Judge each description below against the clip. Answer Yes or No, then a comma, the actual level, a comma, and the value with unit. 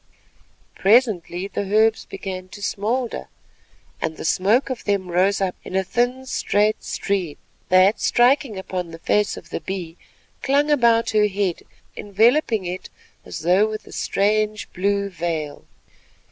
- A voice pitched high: Yes, high, 200 Hz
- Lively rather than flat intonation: No, average, 3.3 semitones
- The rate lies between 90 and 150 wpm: Yes, average, 145 wpm